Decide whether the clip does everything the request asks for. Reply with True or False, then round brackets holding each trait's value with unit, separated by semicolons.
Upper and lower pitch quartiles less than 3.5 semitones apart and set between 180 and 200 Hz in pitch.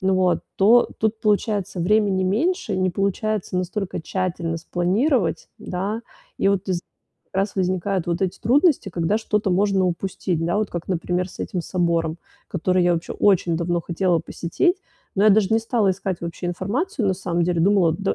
True (2.9 semitones; 190 Hz)